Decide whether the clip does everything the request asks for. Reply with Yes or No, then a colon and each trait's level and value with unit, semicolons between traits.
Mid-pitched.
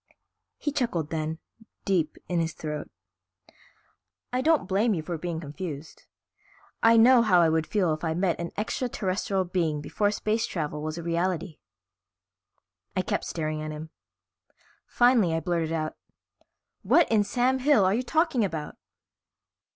Yes: medium, 175 Hz